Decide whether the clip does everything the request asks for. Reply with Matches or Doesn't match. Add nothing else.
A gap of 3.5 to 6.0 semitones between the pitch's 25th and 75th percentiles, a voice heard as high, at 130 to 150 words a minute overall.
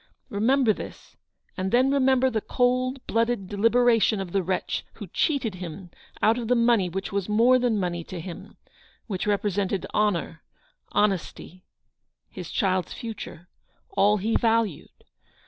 Doesn't match